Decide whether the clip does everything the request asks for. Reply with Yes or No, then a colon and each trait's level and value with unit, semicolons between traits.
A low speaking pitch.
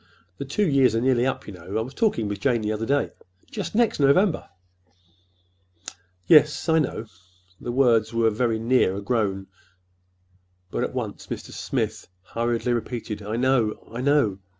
Yes: low, 120 Hz